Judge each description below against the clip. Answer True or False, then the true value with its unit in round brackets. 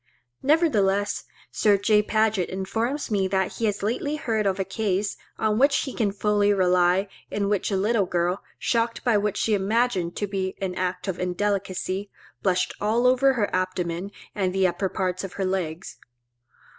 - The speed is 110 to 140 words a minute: False (170 wpm)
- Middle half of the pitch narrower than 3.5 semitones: True (2.7 semitones)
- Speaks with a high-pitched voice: True (200 Hz)